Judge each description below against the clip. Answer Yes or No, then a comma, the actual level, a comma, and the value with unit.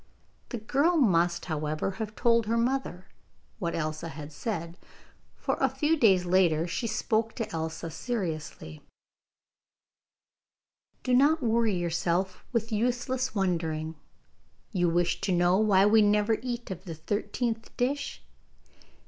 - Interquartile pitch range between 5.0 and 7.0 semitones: Yes, wide, 5.6 semitones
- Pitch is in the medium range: No, high, 205 Hz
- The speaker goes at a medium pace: No, slow, 130 wpm